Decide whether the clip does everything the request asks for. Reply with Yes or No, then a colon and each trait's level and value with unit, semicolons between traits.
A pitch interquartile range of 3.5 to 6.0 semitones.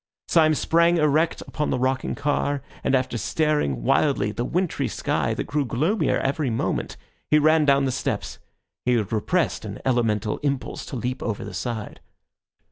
Yes: average, 4.3 semitones